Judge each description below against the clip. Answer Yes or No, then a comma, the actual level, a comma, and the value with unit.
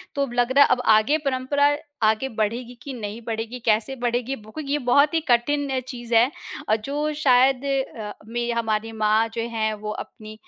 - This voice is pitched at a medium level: No, high, 240 Hz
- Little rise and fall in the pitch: No, average, 3.5 semitones